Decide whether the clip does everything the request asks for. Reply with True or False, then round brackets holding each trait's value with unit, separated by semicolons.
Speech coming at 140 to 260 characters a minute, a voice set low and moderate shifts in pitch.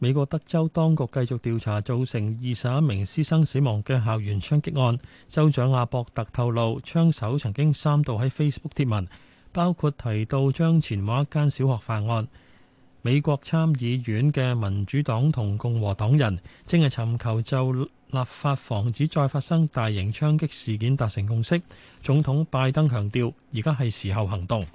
False (270 characters per minute; 130 Hz; 4.6 semitones)